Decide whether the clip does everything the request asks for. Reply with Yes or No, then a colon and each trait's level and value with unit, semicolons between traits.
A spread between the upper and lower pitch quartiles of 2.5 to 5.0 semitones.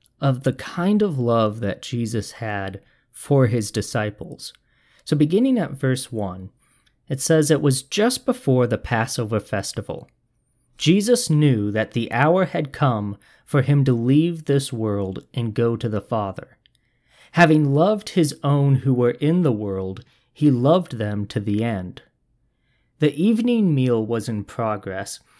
No: wide, 5.4 semitones